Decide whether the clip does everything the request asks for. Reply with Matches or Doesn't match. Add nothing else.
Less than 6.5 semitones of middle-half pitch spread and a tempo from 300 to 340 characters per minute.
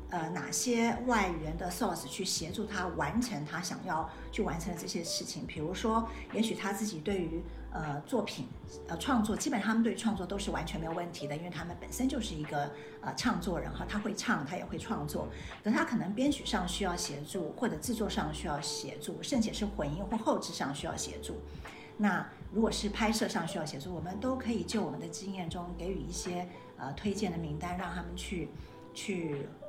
Matches